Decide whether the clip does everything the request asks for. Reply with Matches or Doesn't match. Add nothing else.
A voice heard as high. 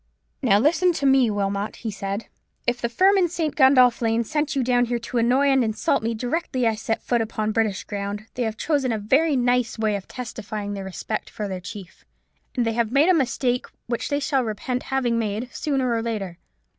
Matches